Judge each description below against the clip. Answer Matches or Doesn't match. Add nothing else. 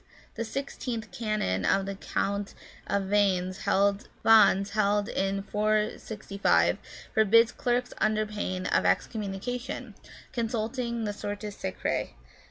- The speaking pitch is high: Matches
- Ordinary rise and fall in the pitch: Doesn't match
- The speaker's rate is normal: Doesn't match